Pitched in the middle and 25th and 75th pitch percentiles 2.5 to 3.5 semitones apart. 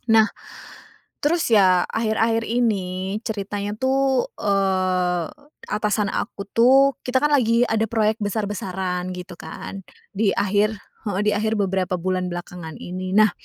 No: high, 205 Hz; average, 3.2 semitones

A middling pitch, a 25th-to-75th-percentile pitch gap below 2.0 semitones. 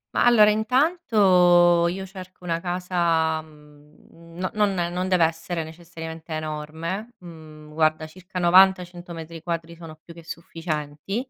No: medium, 170 Hz; narrow, 2.4 semitones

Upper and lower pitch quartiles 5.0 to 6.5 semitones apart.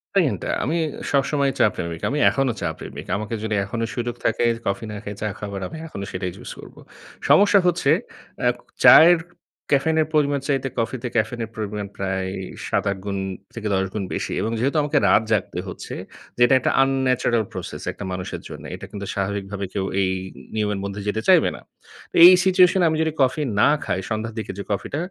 Yes: wide, 5.6 semitones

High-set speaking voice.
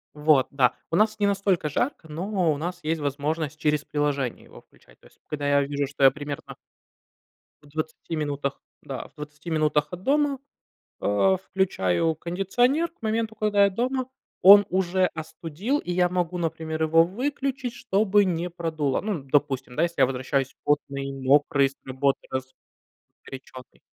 No: medium, 160 Hz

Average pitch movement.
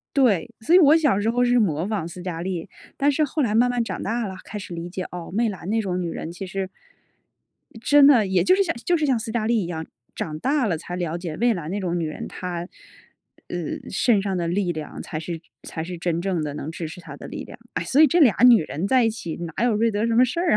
No: wide, 5.8 semitones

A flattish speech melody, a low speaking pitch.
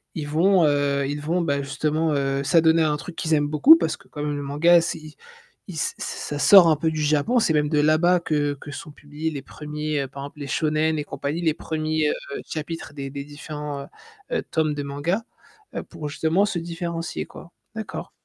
No: narrow, 2.2 semitones; medium, 155 Hz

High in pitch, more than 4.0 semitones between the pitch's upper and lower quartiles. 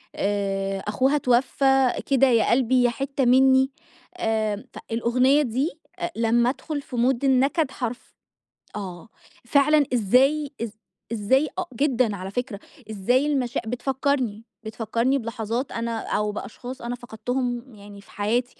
No: high, 245 Hz; average, 3.3 semitones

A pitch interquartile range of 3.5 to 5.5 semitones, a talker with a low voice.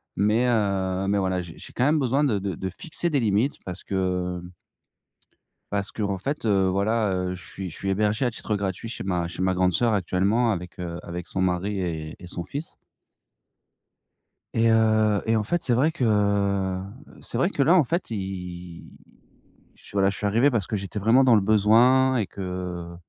Yes: average, 3.8 semitones; low, 100 Hz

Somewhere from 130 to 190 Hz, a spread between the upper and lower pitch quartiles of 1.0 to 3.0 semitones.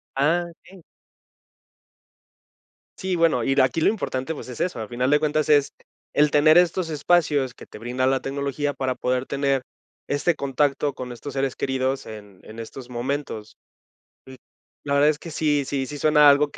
Yes: medium, 140 Hz; narrow, 2.6 semitones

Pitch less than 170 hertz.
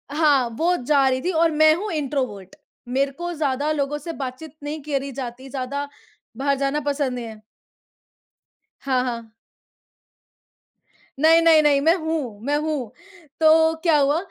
No: very high, 285 Hz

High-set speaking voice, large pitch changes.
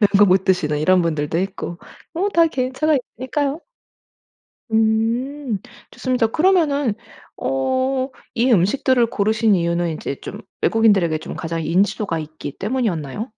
Yes: high, 220 Hz; wide, 7.2 semitones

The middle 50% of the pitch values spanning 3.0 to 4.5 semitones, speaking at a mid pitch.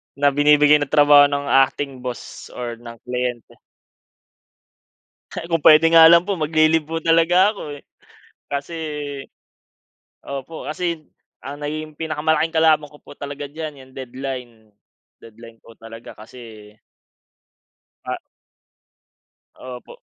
Yes: average, 3.8 semitones; medium, 145 Hz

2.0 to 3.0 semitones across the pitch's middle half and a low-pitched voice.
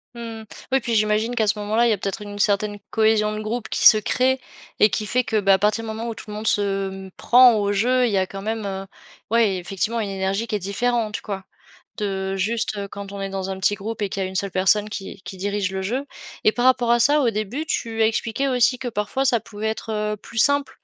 No: average, 2.7 semitones; high, 215 Hz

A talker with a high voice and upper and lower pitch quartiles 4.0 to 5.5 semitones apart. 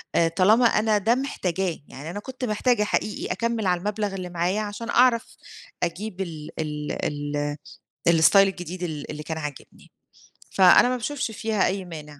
Yes: high, 195 Hz; average, 4.6 semitones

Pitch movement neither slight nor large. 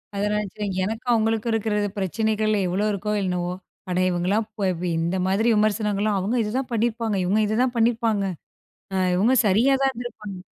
No: narrow, 2.3 semitones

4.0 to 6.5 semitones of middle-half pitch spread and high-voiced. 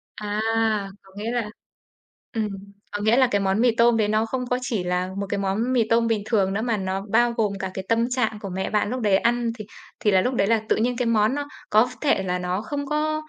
No: average, 3.3 semitones; high, 220 Hz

